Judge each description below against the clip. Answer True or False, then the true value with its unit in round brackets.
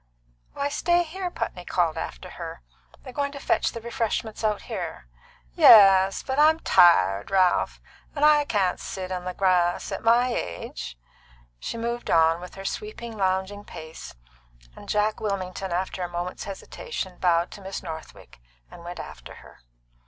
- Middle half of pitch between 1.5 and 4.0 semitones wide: False (5.1 semitones)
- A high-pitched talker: True (195 Hz)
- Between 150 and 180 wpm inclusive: True (160 wpm)